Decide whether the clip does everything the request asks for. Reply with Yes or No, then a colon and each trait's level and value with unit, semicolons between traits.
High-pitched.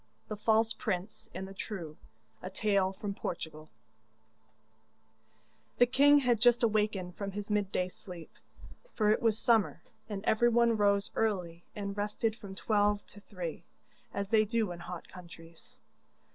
Yes: high, 205 Hz